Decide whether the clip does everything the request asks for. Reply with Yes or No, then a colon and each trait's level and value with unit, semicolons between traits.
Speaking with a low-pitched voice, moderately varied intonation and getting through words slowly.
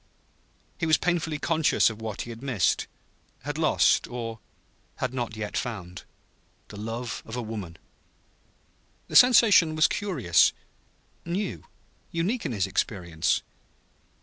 No: low, 120 Hz; wide, 7.0 semitones; slow, 120 wpm